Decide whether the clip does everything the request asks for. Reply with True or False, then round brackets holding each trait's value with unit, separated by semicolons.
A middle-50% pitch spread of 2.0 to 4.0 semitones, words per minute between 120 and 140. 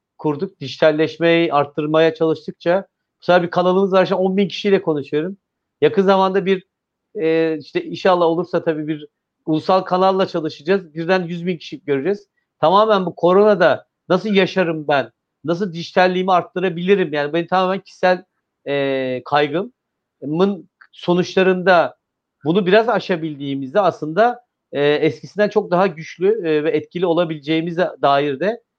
True (3.3 semitones; 125 wpm)